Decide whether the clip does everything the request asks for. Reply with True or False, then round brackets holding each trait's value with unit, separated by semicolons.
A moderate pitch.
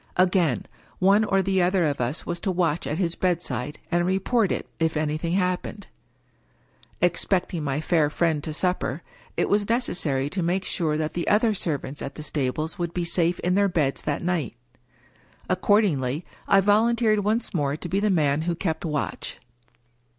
True (175 Hz)